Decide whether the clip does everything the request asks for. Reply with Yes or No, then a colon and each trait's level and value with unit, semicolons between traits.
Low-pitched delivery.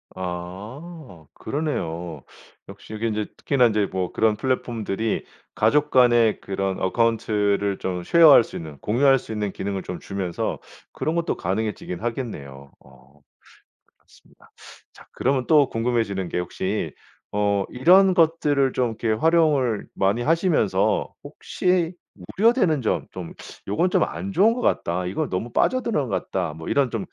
Yes: low, 110 Hz